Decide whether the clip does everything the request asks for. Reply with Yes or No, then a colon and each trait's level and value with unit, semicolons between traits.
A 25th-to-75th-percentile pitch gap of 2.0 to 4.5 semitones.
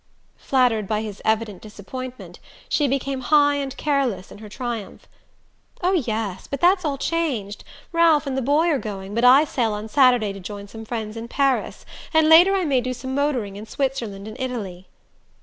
No: average, 4.9 semitones